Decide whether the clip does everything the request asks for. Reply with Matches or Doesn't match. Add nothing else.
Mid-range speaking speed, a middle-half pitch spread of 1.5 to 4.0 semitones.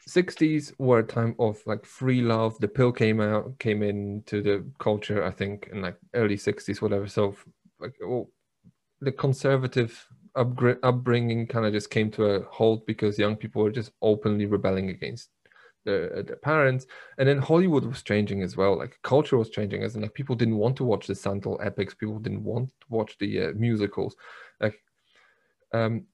Matches